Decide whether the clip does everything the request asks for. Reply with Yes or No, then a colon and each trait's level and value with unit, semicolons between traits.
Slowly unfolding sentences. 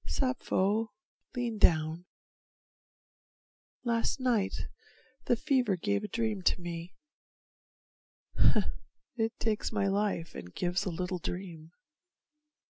Yes: slow, 100 wpm